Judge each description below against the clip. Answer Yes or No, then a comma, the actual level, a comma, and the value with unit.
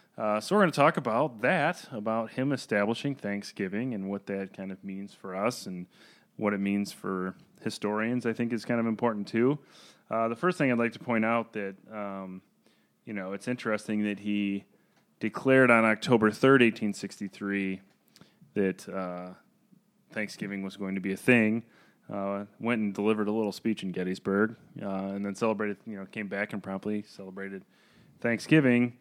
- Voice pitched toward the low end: Yes, low, 105 Hz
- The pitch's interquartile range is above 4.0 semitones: No, average, 3.0 semitones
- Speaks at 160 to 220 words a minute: Yes, average, 180 wpm